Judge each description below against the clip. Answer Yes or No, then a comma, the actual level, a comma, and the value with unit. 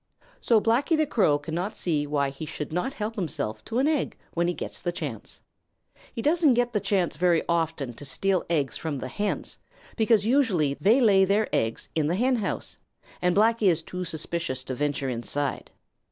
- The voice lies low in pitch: No, medium, 175 Hz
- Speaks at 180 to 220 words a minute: Yes, average, 185 wpm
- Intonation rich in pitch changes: Yes, wide, 7.2 semitones